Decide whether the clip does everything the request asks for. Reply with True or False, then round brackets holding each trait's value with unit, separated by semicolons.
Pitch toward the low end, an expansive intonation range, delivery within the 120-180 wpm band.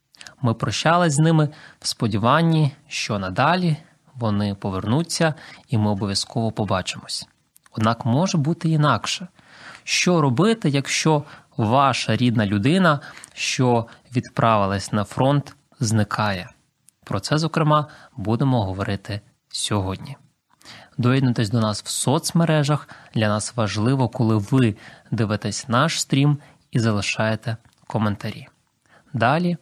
False (125 Hz; 5.7 semitones; 105 wpm)